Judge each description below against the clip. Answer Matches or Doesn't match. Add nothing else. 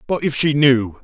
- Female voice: Doesn't match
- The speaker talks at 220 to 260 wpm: Matches